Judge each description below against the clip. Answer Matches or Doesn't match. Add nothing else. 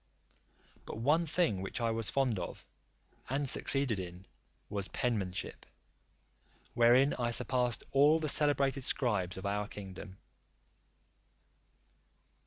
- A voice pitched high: Doesn't match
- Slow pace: Matches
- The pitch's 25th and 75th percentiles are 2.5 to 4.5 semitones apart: Doesn't match